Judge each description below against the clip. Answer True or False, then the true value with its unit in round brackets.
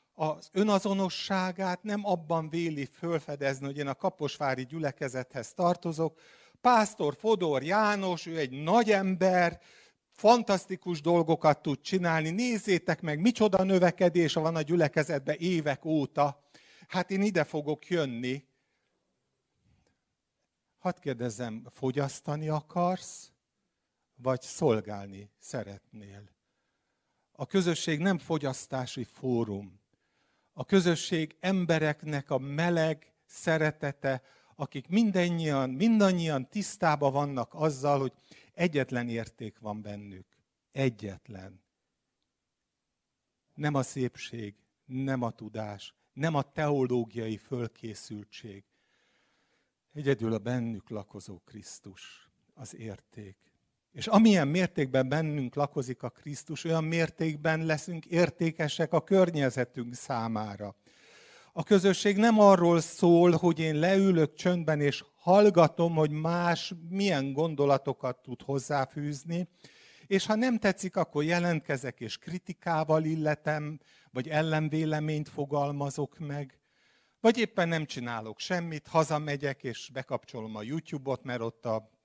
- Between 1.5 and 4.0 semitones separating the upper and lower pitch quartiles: False (5.0 semitones)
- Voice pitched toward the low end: False (150 Hz)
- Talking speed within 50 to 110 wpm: True (105 wpm)